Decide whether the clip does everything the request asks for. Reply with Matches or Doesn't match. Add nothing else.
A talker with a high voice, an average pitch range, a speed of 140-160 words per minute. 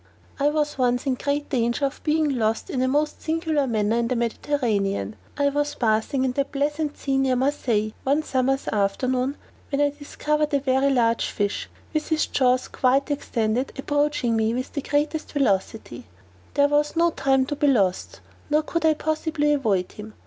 Doesn't match